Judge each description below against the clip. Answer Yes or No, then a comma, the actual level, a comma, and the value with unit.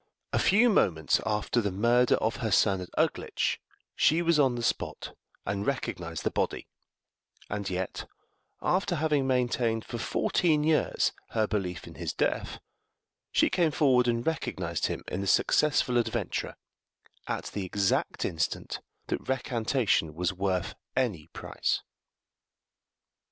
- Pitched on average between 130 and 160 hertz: No, low, 115 Hz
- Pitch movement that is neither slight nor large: No, wide, 6.3 semitones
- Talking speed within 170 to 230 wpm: No, slow, 135 wpm